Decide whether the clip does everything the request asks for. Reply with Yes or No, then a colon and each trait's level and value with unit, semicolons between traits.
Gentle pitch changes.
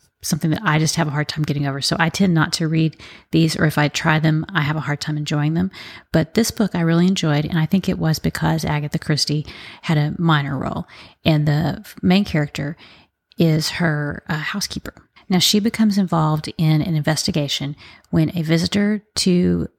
Yes: narrow, 2.2 semitones